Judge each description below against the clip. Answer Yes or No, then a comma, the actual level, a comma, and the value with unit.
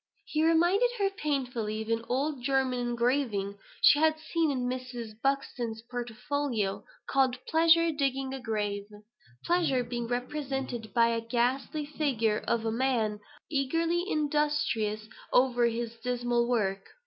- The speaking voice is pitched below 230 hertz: No, very high, 250 Hz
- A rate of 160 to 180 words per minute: No, slow, 135 wpm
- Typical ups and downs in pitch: Yes, average, 4.0 semitones